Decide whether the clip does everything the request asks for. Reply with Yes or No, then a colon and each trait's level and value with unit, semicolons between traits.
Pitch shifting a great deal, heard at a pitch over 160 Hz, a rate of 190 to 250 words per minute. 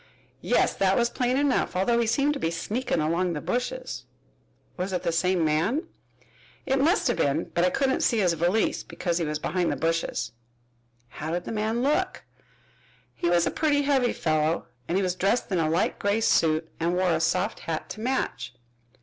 Yes: wide, 6.4 semitones; medium, 185 Hz; average, 195 wpm